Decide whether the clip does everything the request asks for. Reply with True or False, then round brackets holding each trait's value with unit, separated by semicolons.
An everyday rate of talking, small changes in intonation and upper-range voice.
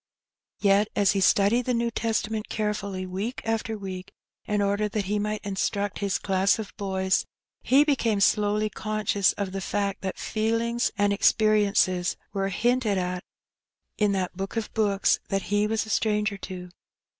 True (160 wpm; 1.8 semitones; 205 Hz)